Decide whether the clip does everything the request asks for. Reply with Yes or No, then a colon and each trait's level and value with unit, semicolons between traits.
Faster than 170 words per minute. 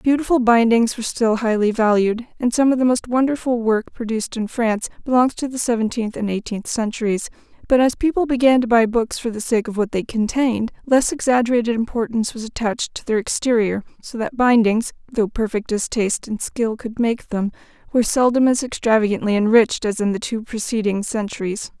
Yes: average, 185 wpm